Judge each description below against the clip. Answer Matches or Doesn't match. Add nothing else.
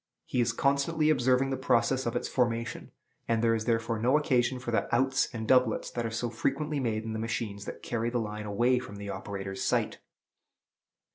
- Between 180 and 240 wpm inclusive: Matches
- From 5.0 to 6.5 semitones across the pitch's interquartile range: Doesn't match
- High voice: Doesn't match